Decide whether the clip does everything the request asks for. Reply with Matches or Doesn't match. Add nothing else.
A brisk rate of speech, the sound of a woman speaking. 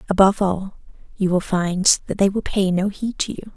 Matches